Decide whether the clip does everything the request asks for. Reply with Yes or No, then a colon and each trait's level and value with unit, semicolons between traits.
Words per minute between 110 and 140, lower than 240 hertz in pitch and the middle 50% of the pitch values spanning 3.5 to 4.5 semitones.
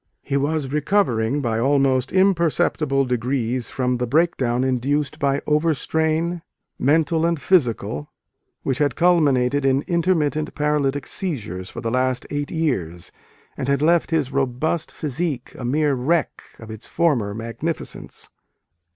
Yes: slow, 135 wpm; medium, 140 Hz; average, 4.2 semitones